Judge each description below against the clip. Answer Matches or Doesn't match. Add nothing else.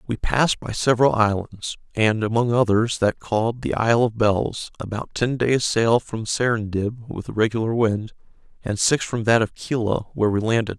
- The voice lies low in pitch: Matches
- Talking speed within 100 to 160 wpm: Doesn't match